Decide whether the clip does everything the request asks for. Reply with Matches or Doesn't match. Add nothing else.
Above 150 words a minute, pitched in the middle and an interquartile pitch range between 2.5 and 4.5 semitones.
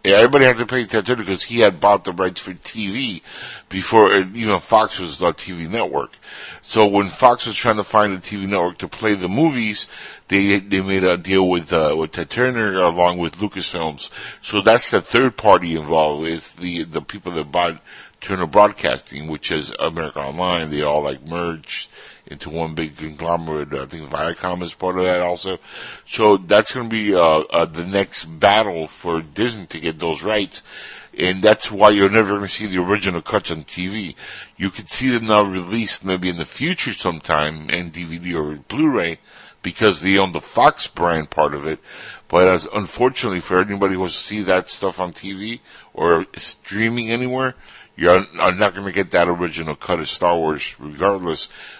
Doesn't match